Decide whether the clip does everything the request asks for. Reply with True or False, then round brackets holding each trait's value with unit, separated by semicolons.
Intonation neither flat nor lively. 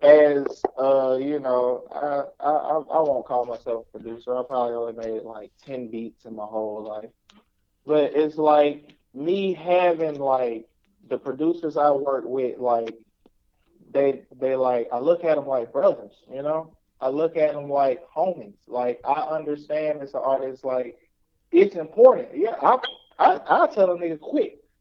True (4.0 semitones)